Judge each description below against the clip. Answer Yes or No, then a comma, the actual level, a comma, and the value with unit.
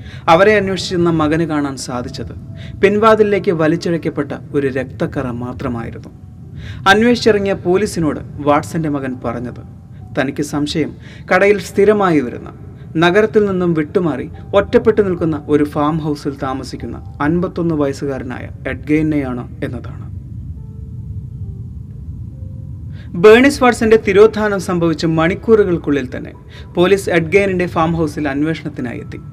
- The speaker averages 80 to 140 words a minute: Yes, average, 90 wpm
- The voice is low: No, medium, 150 Hz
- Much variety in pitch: Yes, wide, 6.6 semitones